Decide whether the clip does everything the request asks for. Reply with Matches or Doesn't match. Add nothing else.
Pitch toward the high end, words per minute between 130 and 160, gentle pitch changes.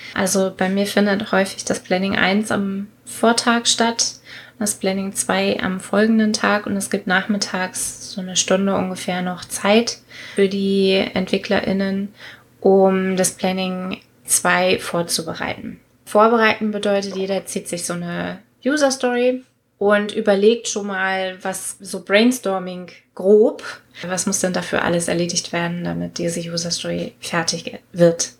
Matches